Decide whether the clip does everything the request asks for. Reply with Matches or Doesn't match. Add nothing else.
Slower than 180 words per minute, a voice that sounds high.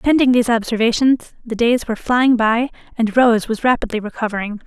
Matches